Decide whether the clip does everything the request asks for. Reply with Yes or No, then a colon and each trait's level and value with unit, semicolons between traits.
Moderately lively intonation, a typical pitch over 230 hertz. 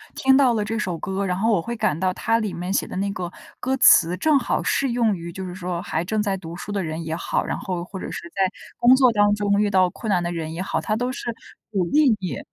No: average, 4.0 semitones; high, 195 Hz